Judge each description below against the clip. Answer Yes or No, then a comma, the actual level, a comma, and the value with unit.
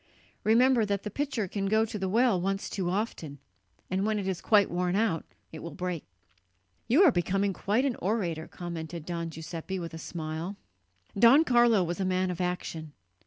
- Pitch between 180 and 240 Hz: Yes, high, 190 Hz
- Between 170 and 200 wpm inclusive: Yes, average, 185 wpm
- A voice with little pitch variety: No, average, 4.1 semitones